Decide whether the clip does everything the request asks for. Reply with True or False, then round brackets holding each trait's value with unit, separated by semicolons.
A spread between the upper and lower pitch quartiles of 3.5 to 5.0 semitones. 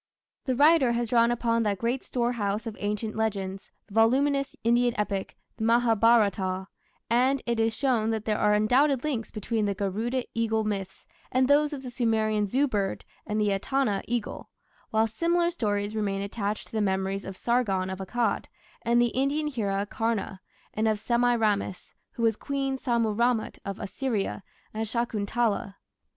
False (2.9 semitones)